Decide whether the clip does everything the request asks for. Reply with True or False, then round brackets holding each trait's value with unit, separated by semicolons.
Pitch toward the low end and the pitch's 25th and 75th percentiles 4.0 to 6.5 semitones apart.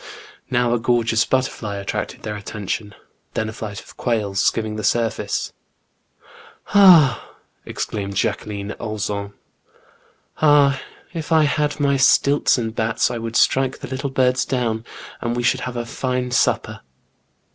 False (120 Hz; 3.5 semitones)